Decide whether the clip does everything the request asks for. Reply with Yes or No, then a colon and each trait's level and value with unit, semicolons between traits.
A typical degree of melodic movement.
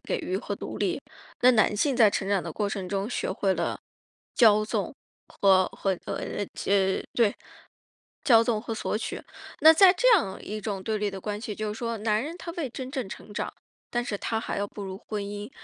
Yes: average, 3.2 semitones